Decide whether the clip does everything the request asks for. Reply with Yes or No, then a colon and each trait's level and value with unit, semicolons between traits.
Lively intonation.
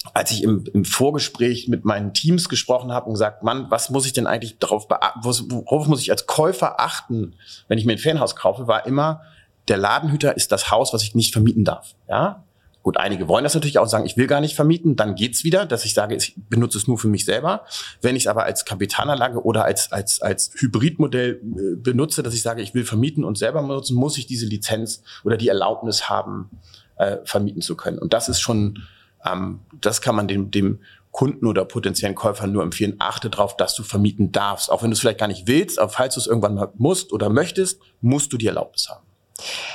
No: average, 3.9 semitones